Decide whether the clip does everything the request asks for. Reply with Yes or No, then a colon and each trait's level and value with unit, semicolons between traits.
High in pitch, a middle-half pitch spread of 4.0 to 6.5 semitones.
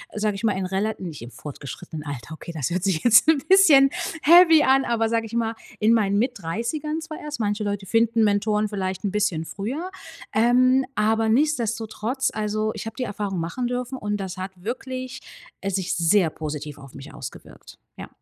Yes: high, 215 Hz; average, 4.7 semitones